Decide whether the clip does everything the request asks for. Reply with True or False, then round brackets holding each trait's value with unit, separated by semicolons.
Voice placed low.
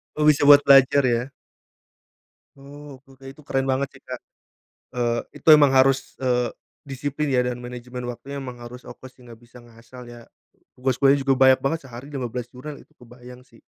True (130 Hz)